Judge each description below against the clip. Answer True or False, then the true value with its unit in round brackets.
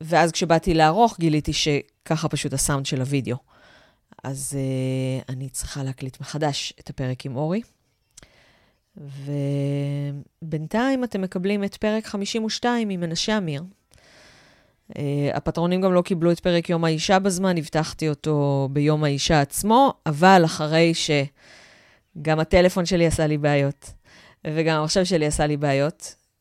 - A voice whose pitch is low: False (155 Hz)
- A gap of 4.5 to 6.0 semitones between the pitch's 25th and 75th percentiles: False (4.1 semitones)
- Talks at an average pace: True (130 wpm)